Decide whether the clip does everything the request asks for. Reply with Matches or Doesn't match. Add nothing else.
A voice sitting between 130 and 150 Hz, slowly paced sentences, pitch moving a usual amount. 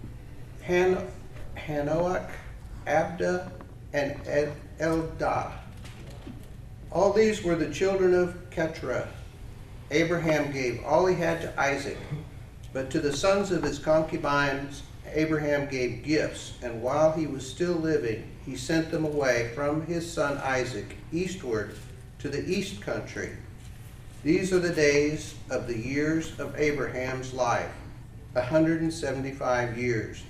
Matches